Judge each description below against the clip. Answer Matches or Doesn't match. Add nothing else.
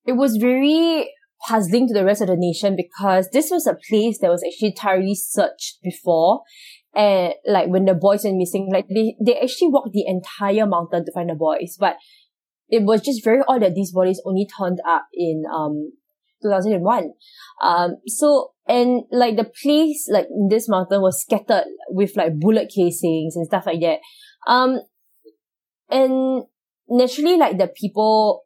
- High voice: Matches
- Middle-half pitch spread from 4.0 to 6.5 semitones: Matches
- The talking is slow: Doesn't match